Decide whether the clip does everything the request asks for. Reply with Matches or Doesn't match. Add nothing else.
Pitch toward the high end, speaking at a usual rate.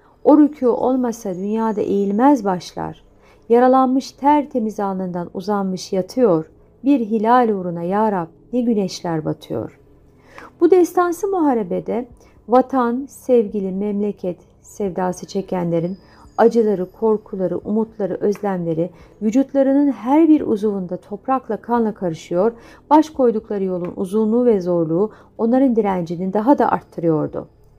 Matches